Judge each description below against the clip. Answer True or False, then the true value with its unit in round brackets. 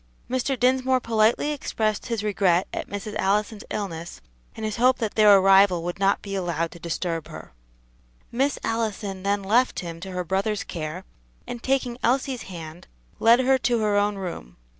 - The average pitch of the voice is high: True (205 Hz)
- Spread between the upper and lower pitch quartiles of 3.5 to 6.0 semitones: True (4.3 semitones)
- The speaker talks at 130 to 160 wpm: False (170 wpm)